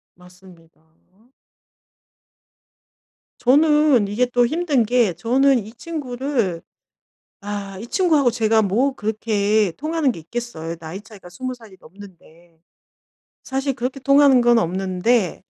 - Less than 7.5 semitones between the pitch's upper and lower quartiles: Yes, wide, 5.6 semitones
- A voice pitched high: Yes, high, 230 Hz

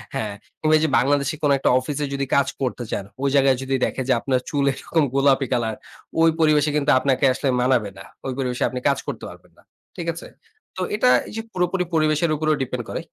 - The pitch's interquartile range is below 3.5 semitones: Yes, average, 3.1 semitones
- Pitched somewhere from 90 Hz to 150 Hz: Yes, medium, 140 Hz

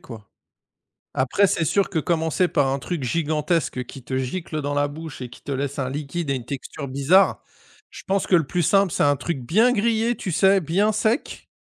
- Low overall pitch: No, medium, 160 Hz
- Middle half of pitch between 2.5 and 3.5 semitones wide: No, wide, 5.6 semitones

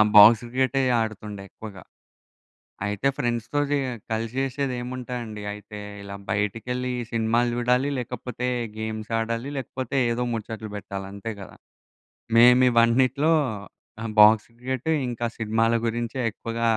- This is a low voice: Yes, low, 115 Hz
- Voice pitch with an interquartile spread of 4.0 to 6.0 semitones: No, narrow, 2.4 semitones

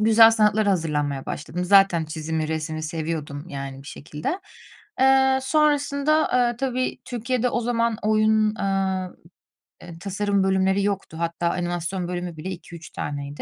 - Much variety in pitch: Yes, wide, 5.8 semitones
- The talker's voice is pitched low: No, high, 190 Hz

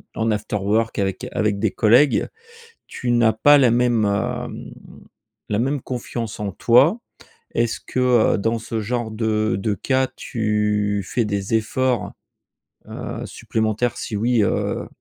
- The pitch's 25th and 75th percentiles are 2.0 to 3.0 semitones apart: Yes, narrow, 2.5 semitones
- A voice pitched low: Yes, low, 110 Hz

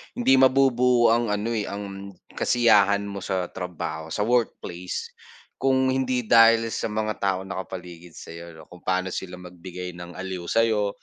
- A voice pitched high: No, low, 100 Hz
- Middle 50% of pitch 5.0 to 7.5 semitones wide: No, average, 4.2 semitones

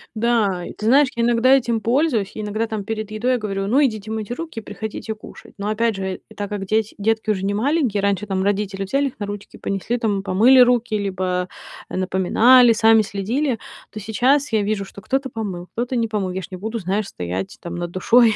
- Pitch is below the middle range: No, high, 215 Hz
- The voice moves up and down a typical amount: Yes, average, 3.1 semitones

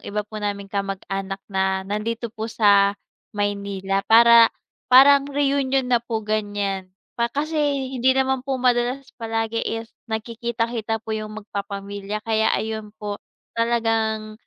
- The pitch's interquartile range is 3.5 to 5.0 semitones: No, narrow, 2.6 semitones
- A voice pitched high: Yes, high, 220 Hz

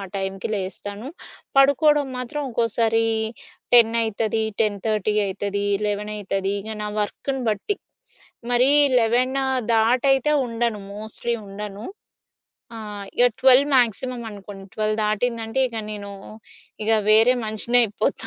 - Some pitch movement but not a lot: Yes, average, 3.0 semitones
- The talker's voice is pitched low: No, high, 220 Hz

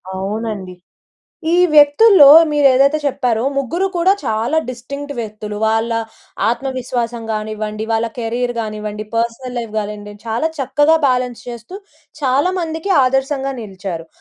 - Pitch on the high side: Yes, high, 240 Hz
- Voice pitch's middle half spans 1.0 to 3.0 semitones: No, average, 4.4 semitones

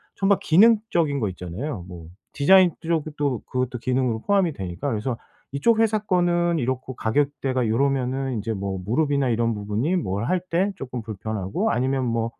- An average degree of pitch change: No, wide, 6.5 semitones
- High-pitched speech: No, low, 130 Hz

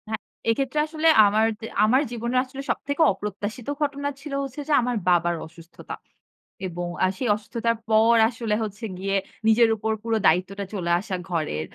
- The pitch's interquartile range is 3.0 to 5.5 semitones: Yes, average, 4.4 semitones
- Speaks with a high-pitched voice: Yes, high, 220 Hz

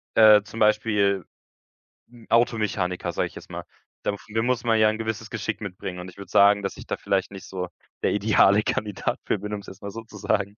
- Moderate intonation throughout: No, narrow, 2.0 semitones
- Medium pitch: No, low, 105 Hz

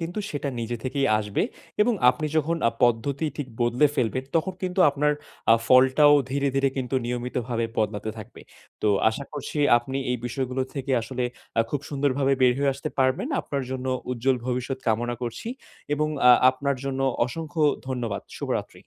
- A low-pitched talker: Yes, low, 130 Hz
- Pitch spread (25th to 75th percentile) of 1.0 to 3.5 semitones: Yes, average, 2.8 semitones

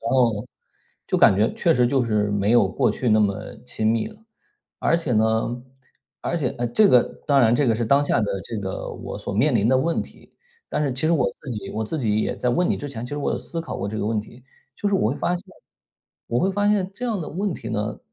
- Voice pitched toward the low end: Yes, low, 120 Hz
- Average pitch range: No, wide, 5.8 semitones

